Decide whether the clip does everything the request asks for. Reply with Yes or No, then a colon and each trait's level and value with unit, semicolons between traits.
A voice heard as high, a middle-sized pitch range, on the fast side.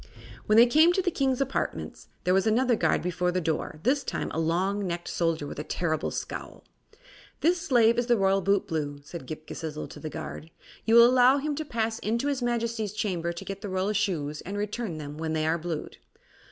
No: high, 195 Hz; wide, 6.6 semitones; fast, 215 wpm